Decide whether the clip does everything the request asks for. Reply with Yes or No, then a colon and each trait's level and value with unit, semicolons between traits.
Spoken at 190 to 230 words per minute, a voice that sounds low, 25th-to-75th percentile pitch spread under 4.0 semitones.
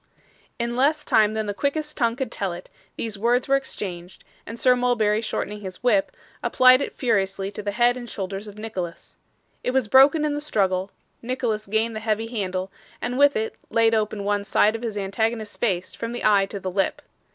No: average, 200 wpm; high, 220 Hz; average, 3.5 semitones